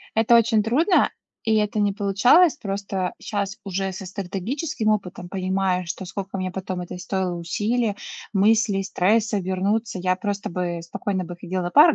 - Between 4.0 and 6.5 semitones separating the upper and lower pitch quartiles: No, average, 2.9 semitones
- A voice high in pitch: Yes, high, 195 Hz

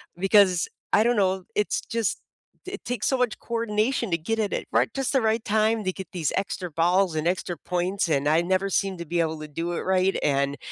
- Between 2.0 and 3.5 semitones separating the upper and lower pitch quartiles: No, average, 4.2 semitones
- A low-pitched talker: No, high, 190 Hz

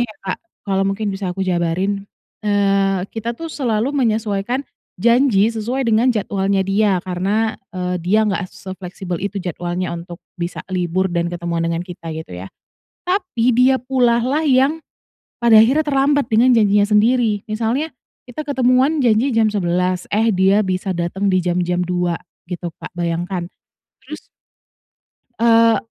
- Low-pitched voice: No, high, 200 Hz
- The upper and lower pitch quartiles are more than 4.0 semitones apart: Yes, average, 4.5 semitones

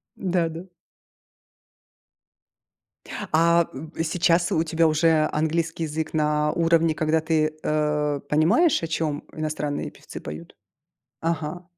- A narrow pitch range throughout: Yes, narrow, 1.6 semitones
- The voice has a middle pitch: Yes, medium, 160 Hz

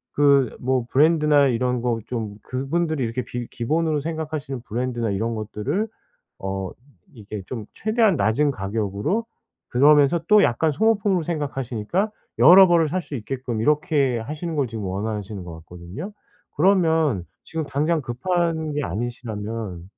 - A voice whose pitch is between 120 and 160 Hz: Yes, low, 135 Hz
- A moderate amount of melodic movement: No, wide, 6.0 semitones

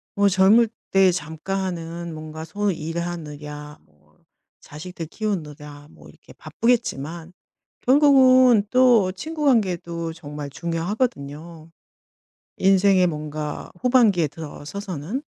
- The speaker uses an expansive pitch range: No, average, 5.0 semitones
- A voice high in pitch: No, medium, 170 Hz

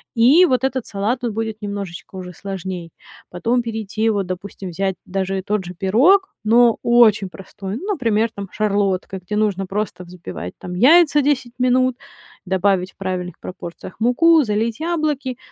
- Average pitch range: Yes, average, 4.5 semitones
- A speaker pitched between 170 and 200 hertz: No, high, 210 Hz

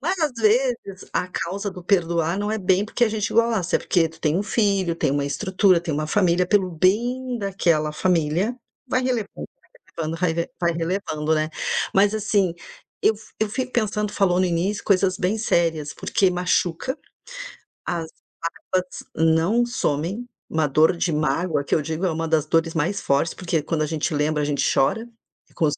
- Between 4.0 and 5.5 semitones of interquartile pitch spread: Yes, average, 4.4 semitones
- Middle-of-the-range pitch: Yes, medium, 180 Hz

